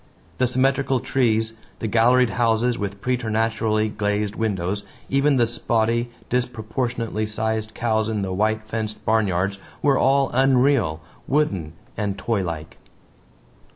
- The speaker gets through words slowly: Yes, slow, 120 wpm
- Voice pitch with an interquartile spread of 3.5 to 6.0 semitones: No, average, 2.8 semitones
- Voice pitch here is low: Yes, low, 110 Hz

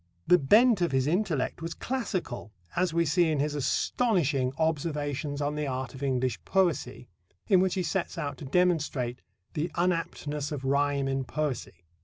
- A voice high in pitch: No, medium, 150 Hz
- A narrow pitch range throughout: No, average, 4.4 semitones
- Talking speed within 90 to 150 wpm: No, average, 165 wpm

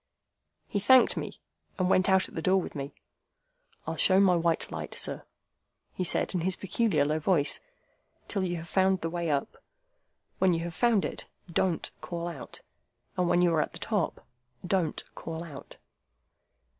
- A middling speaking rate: Yes, average, 175 wpm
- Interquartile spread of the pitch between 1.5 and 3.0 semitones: Yes, narrow, 2.5 semitones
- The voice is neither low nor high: Yes, medium, 175 Hz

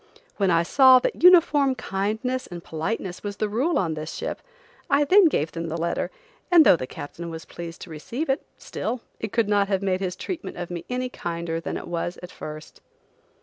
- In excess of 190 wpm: Yes, fast, 205 wpm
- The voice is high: Yes, high, 195 Hz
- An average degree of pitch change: No, wide, 7.2 semitones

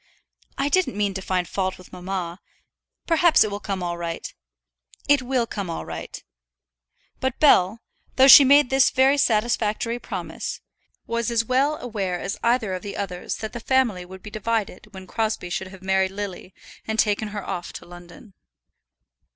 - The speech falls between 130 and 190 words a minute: Yes, average, 170 wpm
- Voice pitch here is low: No, high, 210 Hz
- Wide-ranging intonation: No, average, 4.5 semitones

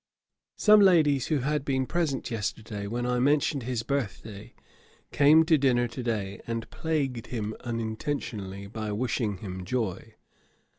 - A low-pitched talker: Yes, low, 120 Hz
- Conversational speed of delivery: Yes, average, 145 wpm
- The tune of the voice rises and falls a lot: No, average, 4.6 semitones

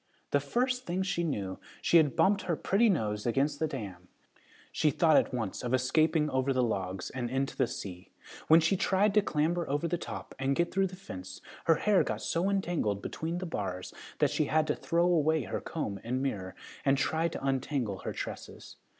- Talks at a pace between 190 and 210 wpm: Yes, average, 200 wpm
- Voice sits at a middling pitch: Yes, medium, 150 Hz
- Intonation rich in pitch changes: Yes, wide, 6.1 semitones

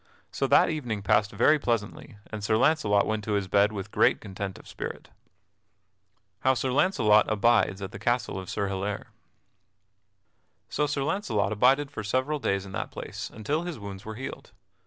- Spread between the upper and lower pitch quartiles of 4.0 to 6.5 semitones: Yes, average, 4.5 semitones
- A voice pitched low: Yes, low, 105 Hz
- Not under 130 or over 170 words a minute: No, average, 180 wpm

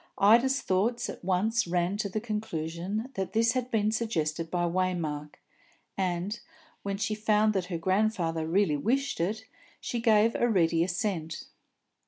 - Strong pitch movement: No, average, 4.3 semitones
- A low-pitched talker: No, high, 195 Hz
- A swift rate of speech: No, average, 145 wpm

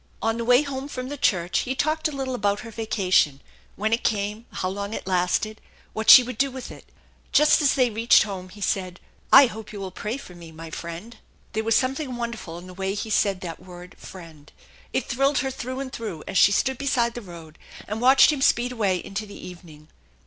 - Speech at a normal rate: No, fast, 225 wpm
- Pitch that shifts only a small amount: No, wide, 5.5 semitones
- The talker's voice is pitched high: Yes, high, 220 Hz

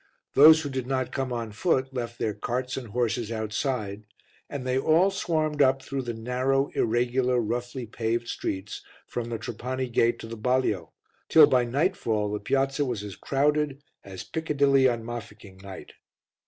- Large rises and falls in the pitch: No, average, 3.1 semitones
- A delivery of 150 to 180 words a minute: Yes, average, 165 wpm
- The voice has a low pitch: Yes, low, 125 Hz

